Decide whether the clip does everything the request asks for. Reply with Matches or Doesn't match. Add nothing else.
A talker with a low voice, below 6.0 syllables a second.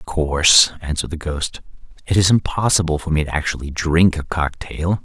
Matches